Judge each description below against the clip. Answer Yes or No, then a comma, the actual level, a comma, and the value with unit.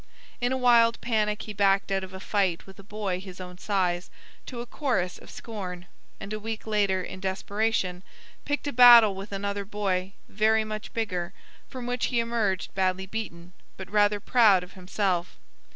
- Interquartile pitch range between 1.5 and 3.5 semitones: Yes, average, 2.8 semitones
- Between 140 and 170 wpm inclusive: No, average, 180 wpm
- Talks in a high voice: Yes, high, 200 Hz